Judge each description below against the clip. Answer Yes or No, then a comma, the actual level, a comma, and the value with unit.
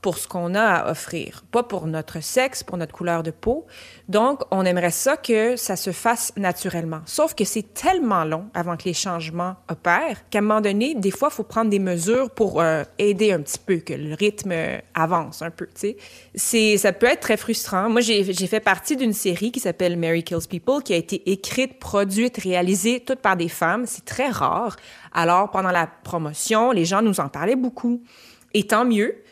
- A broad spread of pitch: No, average, 4.7 semitones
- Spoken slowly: No, average, 210 wpm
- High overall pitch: Yes, high, 195 Hz